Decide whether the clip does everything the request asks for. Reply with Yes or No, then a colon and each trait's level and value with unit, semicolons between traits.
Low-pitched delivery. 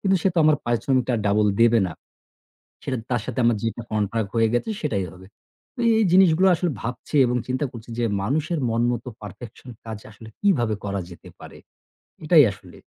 Yes: low, 120 Hz